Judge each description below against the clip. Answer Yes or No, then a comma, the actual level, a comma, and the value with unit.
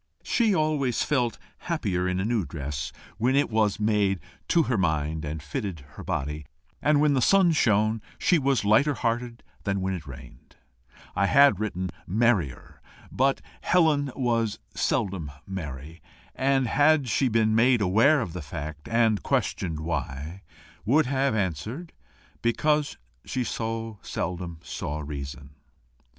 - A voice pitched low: Yes, low, 110 Hz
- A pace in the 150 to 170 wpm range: No, average, 140 wpm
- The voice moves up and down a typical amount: No, wide, 7.7 semitones